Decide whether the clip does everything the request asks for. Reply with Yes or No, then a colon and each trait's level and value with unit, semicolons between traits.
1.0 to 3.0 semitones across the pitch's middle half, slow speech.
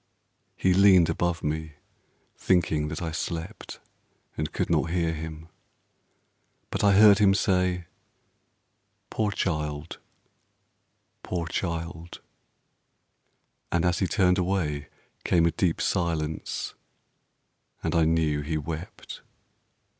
Yes: narrow, 2.5 semitones; slow, 110 wpm